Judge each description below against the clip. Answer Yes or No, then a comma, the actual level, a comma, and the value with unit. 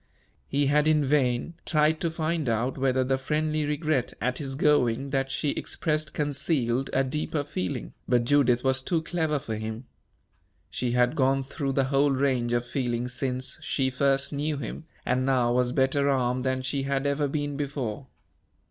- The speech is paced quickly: No, average, 175 wpm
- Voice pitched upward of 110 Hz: Yes, low, 135 Hz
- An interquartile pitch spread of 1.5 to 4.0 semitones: Yes, narrow, 2.6 semitones